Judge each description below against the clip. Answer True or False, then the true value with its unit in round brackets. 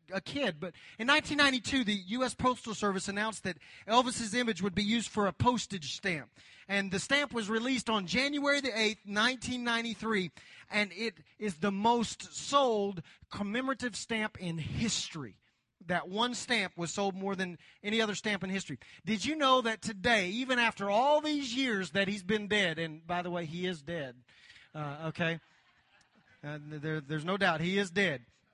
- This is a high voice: True (205 Hz)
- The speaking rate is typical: True (175 wpm)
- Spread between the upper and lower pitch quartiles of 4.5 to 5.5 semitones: True (5.0 semitones)